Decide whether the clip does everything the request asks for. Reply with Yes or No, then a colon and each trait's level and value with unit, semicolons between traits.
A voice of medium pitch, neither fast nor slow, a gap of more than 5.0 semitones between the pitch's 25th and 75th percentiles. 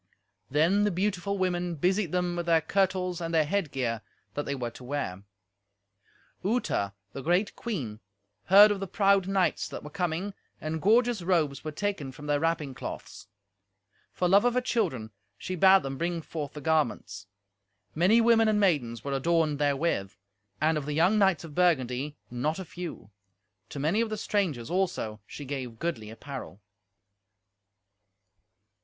Yes: medium, 165 Hz; average, 160 wpm; wide, 5.5 semitones